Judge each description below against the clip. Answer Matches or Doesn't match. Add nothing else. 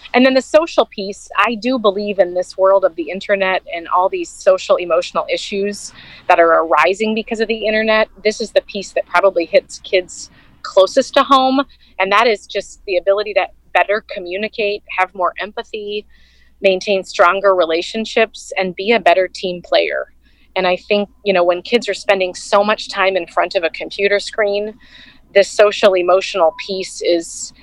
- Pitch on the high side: Matches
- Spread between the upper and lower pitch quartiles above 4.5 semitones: Doesn't match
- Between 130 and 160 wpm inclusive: Doesn't match